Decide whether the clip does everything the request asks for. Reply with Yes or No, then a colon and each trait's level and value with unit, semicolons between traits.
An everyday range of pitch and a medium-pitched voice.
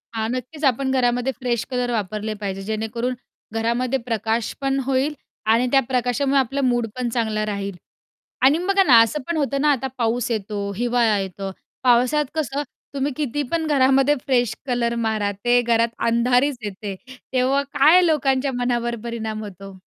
No: average, 3.3 semitones; high, 245 Hz